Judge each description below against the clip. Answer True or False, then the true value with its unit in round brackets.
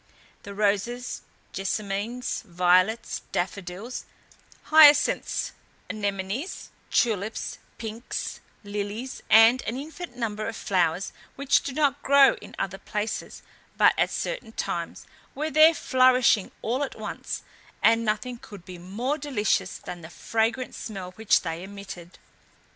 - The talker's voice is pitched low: False (220 Hz)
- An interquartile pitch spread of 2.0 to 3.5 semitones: False (4.7 semitones)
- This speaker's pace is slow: True (120 wpm)